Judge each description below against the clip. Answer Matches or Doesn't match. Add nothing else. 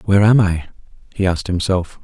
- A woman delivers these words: Doesn't match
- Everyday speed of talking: Matches